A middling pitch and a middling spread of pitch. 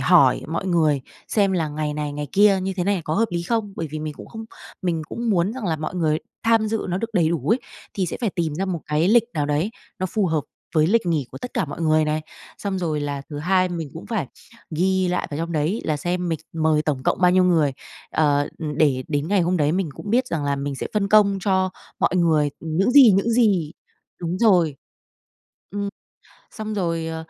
Yes: medium, 170 Hz; average, 4.2 semitones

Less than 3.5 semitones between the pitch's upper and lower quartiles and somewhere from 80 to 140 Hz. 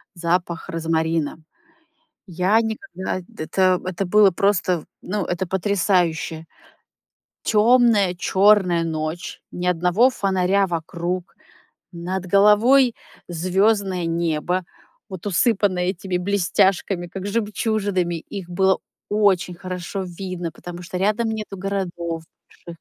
No: average, 2.7 semitones; medium, 185 Hz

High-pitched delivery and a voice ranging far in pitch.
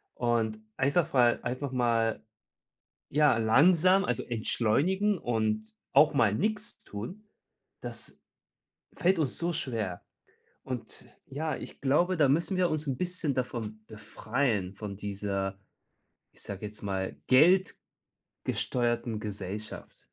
No: low, 120 Hz; wide, 6.2 semitones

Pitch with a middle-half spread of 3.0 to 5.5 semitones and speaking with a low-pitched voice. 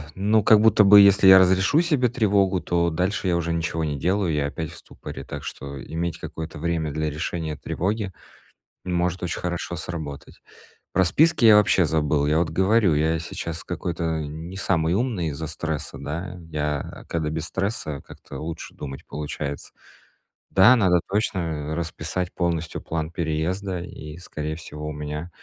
Yes: average, 3.5 semitones; very low, 85 Hz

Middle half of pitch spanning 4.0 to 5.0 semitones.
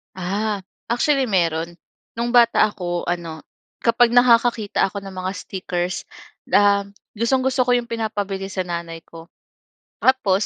Yes: average, 4.6 semitones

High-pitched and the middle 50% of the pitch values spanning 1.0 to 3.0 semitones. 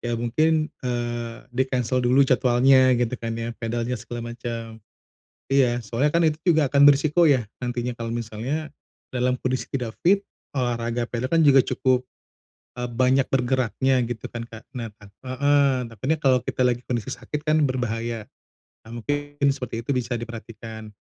No: low, 125 Hz; narrow, 2.6 semitones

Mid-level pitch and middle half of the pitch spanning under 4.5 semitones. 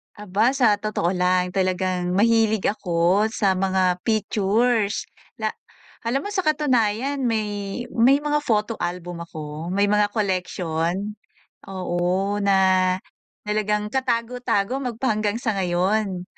No: high, 205 Hz; average, 3.6 semitones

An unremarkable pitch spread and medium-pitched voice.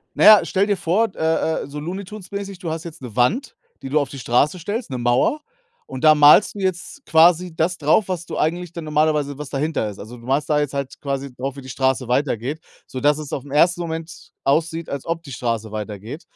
Yes: average, 4.4 semitones; medium, 150 Hz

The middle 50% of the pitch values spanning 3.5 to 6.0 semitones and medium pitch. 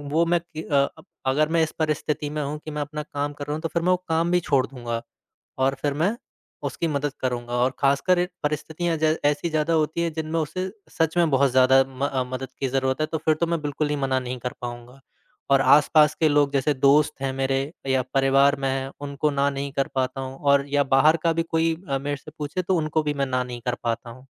No: average, 2.7 semitones; medium, 145 Hz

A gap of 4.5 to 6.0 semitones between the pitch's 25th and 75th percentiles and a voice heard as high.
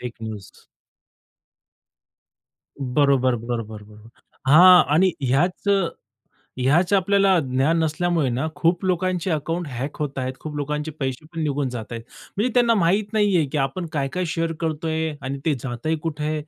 No: average, 4.9 semitones; medium, 155 Hz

